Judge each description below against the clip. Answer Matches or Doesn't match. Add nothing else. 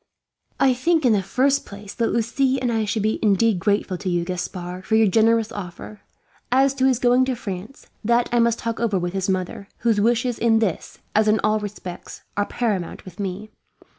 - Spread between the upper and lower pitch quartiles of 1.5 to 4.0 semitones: Matches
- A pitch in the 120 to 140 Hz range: Doesn't match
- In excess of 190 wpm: Matches